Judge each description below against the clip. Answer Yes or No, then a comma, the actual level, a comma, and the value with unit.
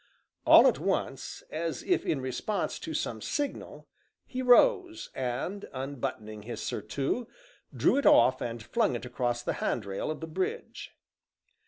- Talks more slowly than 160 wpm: Yes, average, 145 wpm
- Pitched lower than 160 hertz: Yes, low, 135 Hz